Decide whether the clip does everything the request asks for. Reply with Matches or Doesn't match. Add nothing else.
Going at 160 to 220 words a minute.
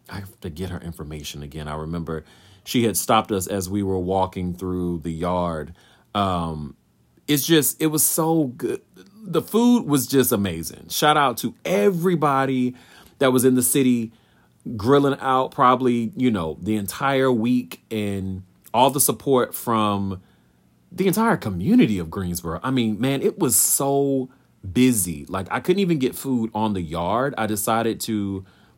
Matches